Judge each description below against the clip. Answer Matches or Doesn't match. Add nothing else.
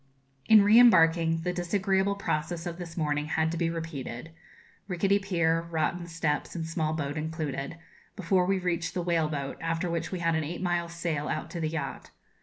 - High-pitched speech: Doesn't match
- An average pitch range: Doesn't match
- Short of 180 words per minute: Doesn't match